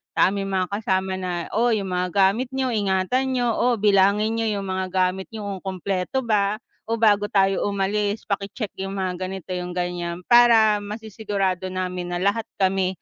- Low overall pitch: No, high, 195 Hz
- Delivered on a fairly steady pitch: Yes, narrow, 2.3 semitones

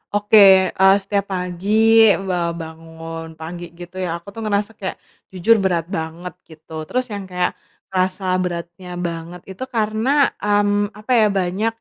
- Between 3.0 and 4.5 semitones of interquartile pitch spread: Yes, average, 3.3 semitones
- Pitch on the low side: No, medium, 185 Hz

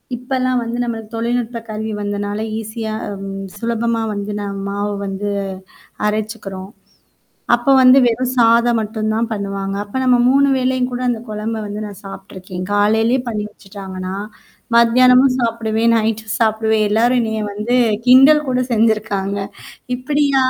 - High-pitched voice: Yes, high, 220 Hz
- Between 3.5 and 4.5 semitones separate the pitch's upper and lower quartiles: No, average, 2.9 semitones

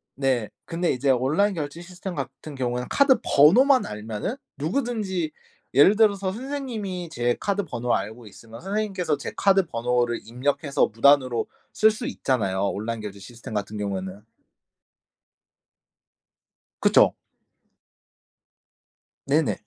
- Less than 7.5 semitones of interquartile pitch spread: No, wide, 8.8 semitones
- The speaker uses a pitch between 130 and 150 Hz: Yes, medium, 140 Hz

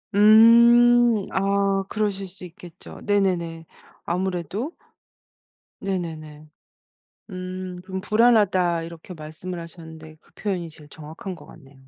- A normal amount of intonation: Yes, average, 3.5 semitones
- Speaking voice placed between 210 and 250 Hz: No, medium, 185 Hz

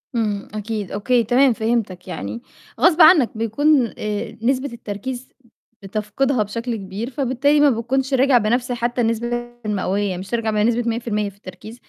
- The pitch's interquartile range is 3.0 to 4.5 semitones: Yes, average, 3.4 semitones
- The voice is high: Yes, high, 230 Hz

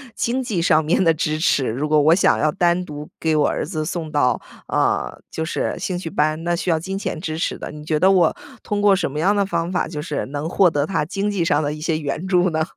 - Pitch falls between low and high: Yes, medium, 165 Hz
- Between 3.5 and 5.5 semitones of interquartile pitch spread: No, average, 3.1 semitones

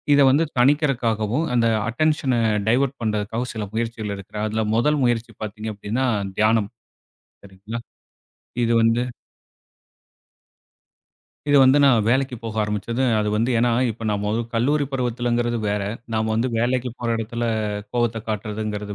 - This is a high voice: No, low, 115 Hz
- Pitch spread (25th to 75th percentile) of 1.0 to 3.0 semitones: Yes, narrow, 2.6 semitones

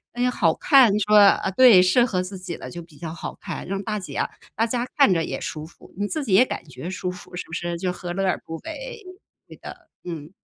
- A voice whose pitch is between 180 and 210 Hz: Yes, medium, 185 Hz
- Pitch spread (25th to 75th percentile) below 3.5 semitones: No, average, 4.4 semitones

